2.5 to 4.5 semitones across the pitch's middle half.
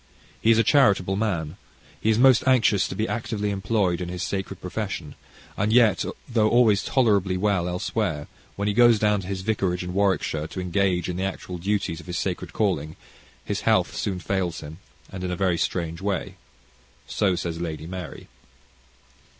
Yes: average, 3.1 semitones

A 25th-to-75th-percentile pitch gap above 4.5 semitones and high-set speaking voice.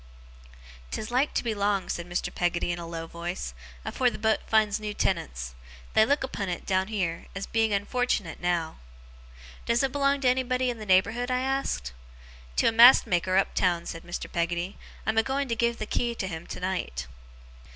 Yes: wide, 5.6 semitones; high, 205 Hz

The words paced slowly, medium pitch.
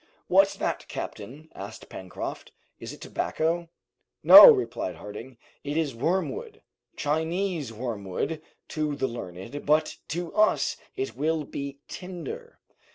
Yes: slow, 120 wpm; medium, 155 Hz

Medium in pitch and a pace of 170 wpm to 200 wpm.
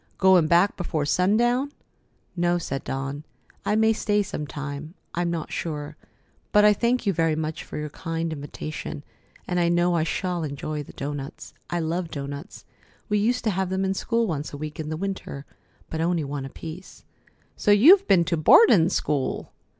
Yes: medium, 170 Hz; average, 180 wpm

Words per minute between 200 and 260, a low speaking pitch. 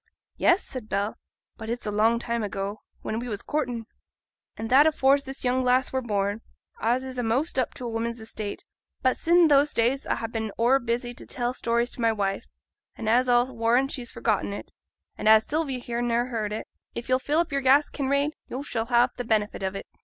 No: fast, 205 wpm; high, 240 Hz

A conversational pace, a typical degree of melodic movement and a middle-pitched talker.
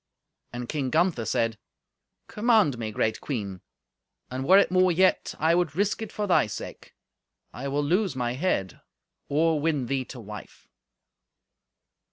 No: average, 150 wpm; wide, 7.1 semitones; medium, 145 Hz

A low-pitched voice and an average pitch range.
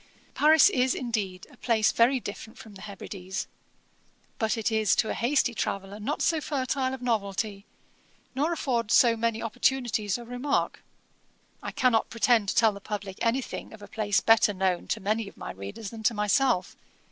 No: high, 225 Hz; average, 3.4 semitones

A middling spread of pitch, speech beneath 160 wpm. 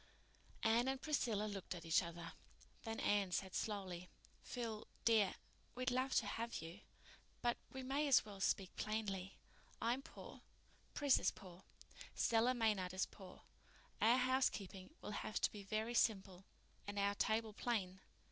Yes: average, 3.8 semitones; average, 140 wpm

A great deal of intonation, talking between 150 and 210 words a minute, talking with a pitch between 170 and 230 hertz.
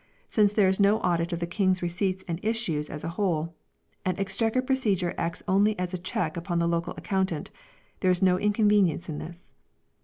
No: average, 3.1 semitones; average, 190 wpm; medium, 185 Hz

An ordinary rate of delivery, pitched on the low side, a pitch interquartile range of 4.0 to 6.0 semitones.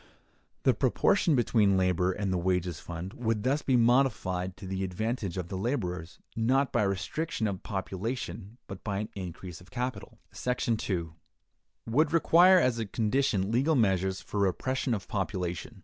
Yes: average, 160 wpm; low, 100 Hz; average, 4.9 semitones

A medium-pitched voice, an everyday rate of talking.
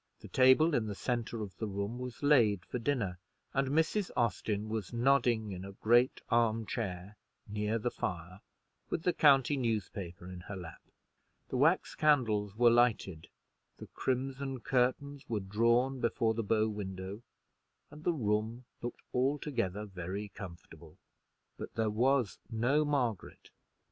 No: low, 115 Hz; average, 145 wpm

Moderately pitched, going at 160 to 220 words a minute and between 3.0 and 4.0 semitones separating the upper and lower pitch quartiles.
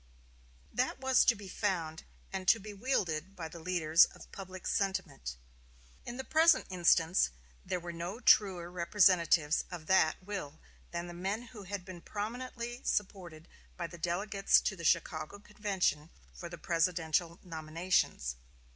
No: medium, 180 Hz; average, 145 wpm; average, 3.4 semitones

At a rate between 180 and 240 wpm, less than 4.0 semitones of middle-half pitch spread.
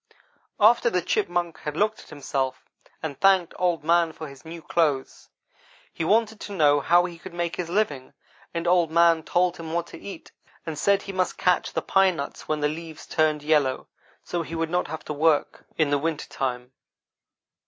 Yes: average, 195 wpm; average, 2.9 semitones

